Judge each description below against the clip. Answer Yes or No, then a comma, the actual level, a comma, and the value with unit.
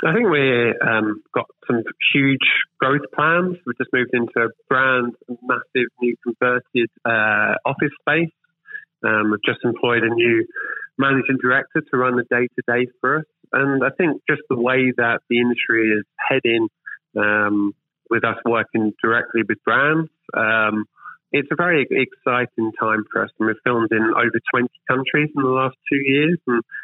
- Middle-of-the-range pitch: No, low, 125 Hz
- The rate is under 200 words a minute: Yes, average, 170 wpm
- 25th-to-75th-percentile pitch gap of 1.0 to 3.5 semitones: Yes, average, 2.9 semitones